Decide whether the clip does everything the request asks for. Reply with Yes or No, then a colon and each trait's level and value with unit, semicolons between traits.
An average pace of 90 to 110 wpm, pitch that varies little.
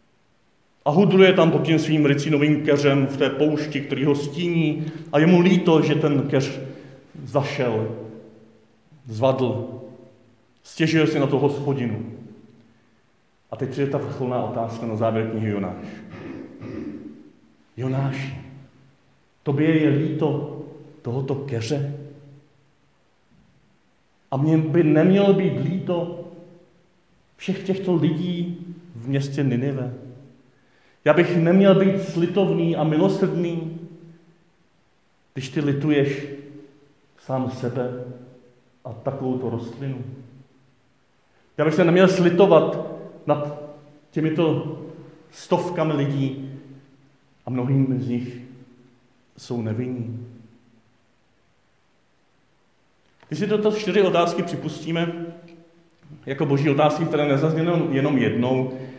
No: slow, 100 wpm; average, 3.9 semitones